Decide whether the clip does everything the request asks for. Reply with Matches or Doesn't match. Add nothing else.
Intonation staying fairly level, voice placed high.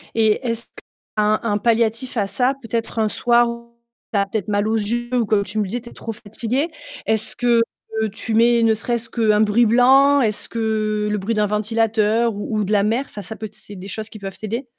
Matches